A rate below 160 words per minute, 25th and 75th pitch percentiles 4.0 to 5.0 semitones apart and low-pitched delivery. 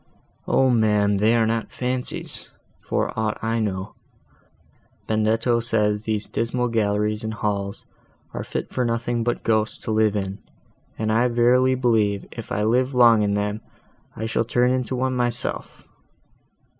No: average, 150 wpm; narrow, 2.4 semitones; low, 110 Hz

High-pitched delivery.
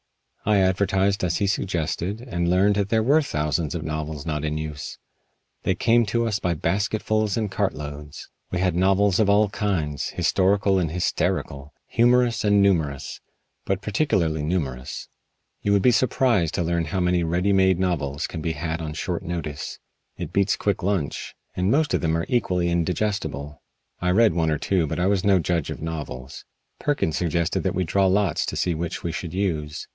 No: very low, 90 Hz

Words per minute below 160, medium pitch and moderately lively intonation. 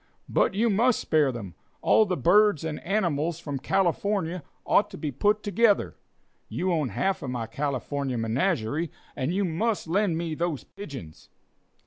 No: average, 150 wpm; medium, 170 Hz; wide, 6.1 semitones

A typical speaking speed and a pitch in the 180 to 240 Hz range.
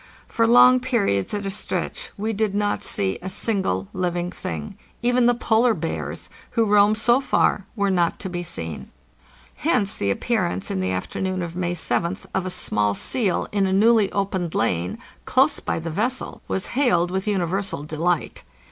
Yes: average, 175 wpm; high, 190 Hz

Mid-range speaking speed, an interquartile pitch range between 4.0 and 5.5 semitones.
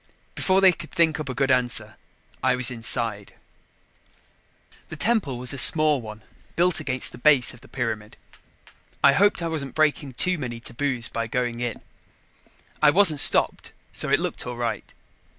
Yes: average, 170 wpm; average, 4.4 semitones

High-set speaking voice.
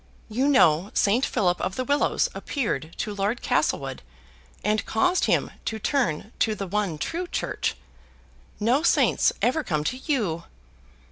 Yes: high, 215 Hz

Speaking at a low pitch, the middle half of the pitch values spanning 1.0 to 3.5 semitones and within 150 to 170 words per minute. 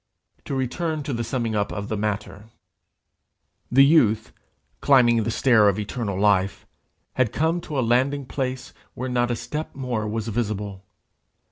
No: low, 120 Hz; average, 3.9 semitones; average, 155 wpm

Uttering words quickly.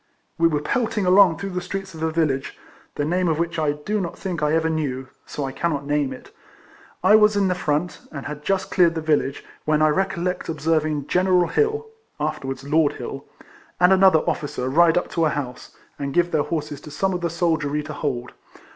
Yes: fast, 210 wpm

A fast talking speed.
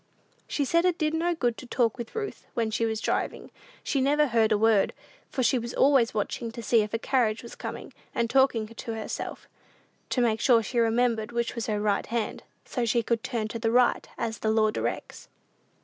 Yes: fast, 210 wpm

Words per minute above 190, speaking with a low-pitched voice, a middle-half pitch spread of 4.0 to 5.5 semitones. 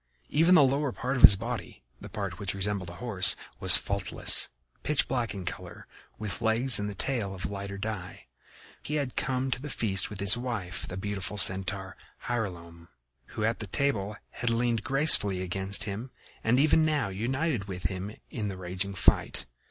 No: average, 175 wpm; low, 105 Hz; average, 4.5 semitones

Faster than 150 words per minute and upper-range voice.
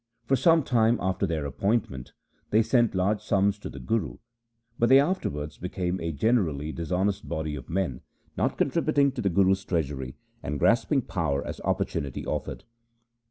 No: average, 160 wpm; very low, 95 Hz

